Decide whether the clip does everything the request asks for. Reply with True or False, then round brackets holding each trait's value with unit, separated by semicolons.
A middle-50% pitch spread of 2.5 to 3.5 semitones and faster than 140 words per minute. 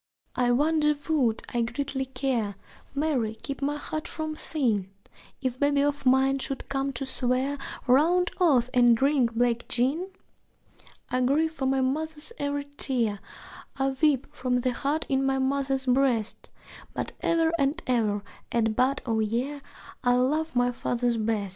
True (2.9 semitones; 155 wpm)